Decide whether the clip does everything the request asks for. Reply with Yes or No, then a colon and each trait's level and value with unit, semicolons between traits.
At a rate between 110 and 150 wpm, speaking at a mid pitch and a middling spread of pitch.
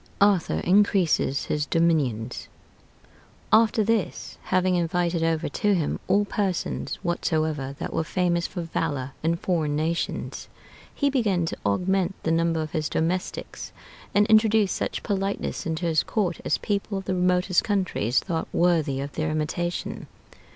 Yes: average, 145 wpm; medium, 175 Hz; average, 3.4 semitones